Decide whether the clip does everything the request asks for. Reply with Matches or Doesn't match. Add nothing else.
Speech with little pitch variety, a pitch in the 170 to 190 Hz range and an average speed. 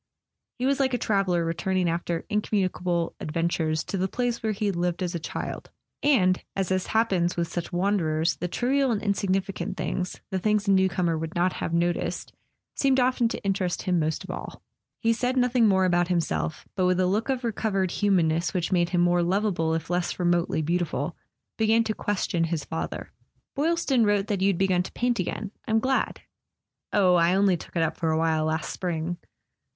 Doesn't match